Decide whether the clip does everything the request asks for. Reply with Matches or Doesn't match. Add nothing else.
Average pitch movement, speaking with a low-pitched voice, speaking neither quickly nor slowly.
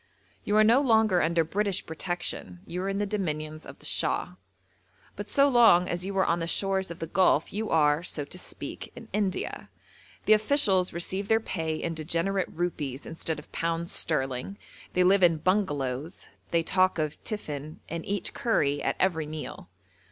Doesn't match